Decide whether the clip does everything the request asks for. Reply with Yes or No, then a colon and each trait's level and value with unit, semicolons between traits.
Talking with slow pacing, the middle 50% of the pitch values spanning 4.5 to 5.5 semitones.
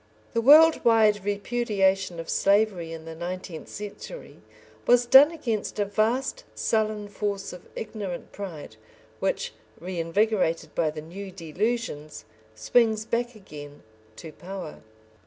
Yes: slow, 120 wpm; average, 4.8 semitones